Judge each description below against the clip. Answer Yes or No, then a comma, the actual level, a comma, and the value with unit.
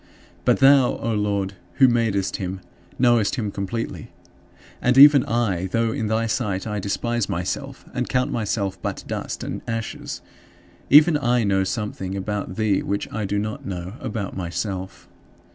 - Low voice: Yes, low, 105 Hz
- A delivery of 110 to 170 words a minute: Yes, average, 155 wpm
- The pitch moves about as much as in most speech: Yes, average, 3.4 semitones